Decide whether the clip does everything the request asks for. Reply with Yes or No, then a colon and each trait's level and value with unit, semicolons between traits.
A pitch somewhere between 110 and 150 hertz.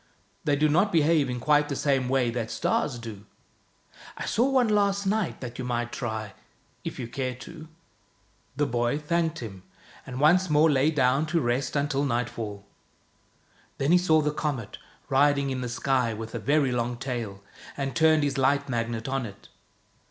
Yes: low, 135 Hz